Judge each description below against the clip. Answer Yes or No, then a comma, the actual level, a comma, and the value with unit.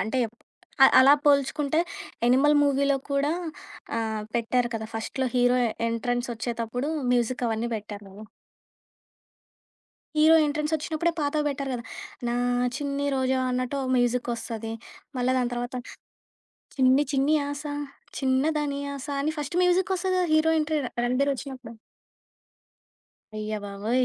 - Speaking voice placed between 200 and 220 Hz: No, very high, 260 Hz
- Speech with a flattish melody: No, average, 3.2 semitones